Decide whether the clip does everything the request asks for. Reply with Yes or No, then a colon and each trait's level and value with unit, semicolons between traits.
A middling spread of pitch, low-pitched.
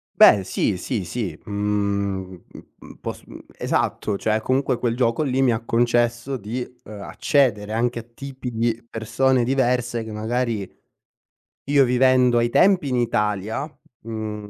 Yes: average, 3.1 semitones; low, 115 Hz